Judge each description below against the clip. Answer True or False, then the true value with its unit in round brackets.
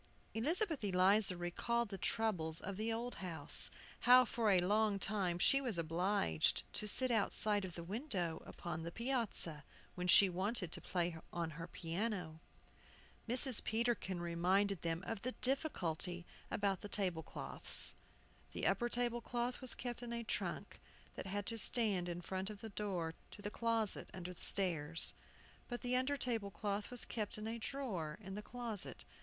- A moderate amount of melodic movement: True (4.9 semitones)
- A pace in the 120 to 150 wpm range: False (170 wpm)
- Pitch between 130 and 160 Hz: False (205 Hz)